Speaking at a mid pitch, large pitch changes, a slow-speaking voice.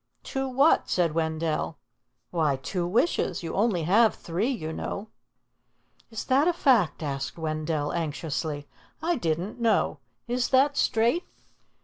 Yes: medium, 180 Hz; wide, 7.4 semitones; slow, 130 wpm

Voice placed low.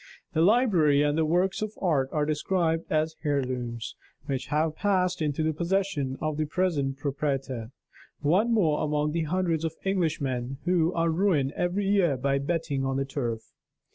No: medium, 155 Hz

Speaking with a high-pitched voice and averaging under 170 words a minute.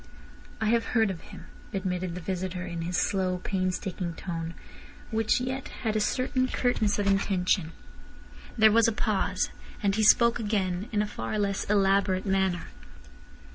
Yes: high, 195 Hz; average, 155 wpm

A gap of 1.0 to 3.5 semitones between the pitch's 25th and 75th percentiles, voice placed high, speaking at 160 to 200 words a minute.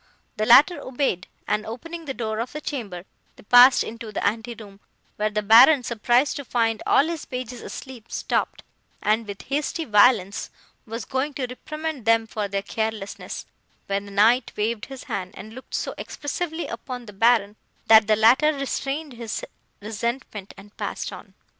No: average, 3.9 semitones; high, 230 Hz; average, 170 wpm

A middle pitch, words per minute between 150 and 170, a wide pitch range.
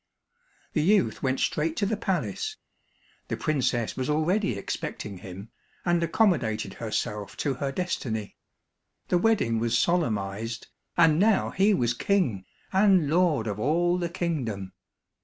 No: medium, 150 Hz; slow, 135 wpm; wide, 8.1 semitones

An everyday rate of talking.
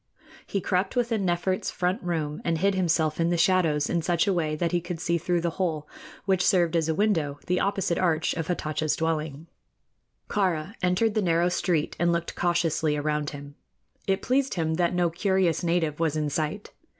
Yes: average, 190 wpm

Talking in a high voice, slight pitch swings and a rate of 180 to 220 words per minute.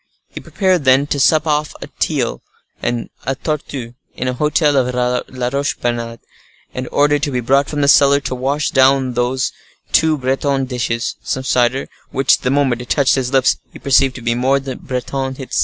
No: low, 130 Hz; narrow, 2.1 semitones; average, 190 wpm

